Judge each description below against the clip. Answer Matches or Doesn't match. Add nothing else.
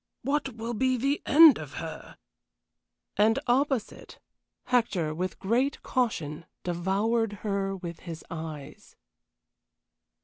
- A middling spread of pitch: Doesn't match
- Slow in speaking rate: Matches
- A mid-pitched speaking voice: Doesn't match